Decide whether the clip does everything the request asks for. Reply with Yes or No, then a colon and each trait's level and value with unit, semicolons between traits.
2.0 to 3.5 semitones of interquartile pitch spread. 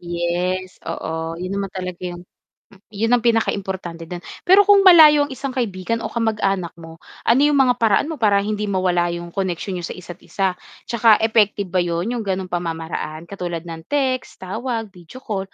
No: average, 4.7 semitones